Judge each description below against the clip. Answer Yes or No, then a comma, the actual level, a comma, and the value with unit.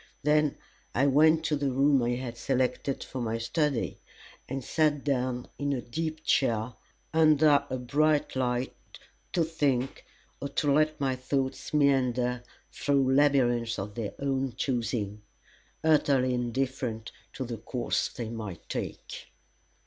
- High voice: No, low, 135 Hz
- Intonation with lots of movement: No, average, 3.0 semitones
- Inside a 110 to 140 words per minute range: Yes, slow, 135 wpm